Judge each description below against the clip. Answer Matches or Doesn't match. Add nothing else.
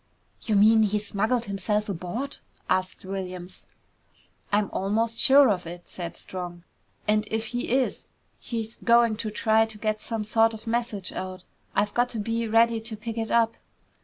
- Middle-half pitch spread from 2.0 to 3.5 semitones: Matches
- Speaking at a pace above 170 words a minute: Doesn't match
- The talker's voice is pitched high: Matches